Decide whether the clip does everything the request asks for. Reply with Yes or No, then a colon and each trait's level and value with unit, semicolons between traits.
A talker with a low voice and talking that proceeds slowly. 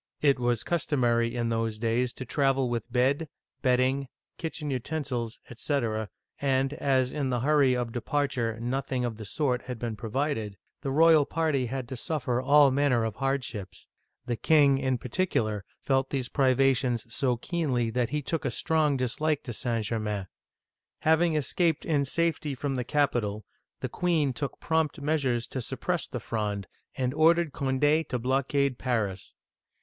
No: low, 130 Hz; average, 160 wpm